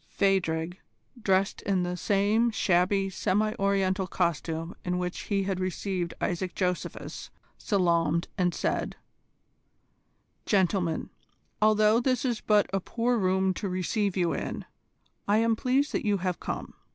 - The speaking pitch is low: No, high, 190 Hz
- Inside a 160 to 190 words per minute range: No, slow, 135 wpm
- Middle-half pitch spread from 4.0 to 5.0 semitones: No, average, 2.7 semitones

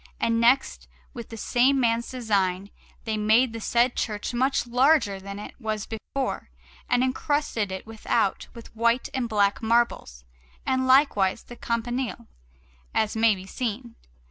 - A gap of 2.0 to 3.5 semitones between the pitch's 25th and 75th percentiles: Yes, average, 2.8 semitones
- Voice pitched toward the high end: Yes, high, 230 Hz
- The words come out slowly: No, average, 145 wpm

